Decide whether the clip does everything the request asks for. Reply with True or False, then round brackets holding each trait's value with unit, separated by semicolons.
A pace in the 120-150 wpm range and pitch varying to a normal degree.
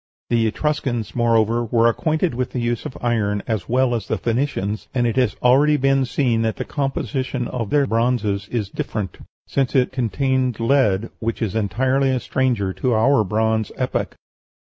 False (170 wpm; 3.0 semitones)